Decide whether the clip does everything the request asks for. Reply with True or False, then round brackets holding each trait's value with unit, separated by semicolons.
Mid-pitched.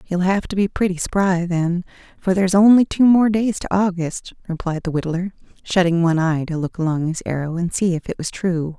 True (180 Hz)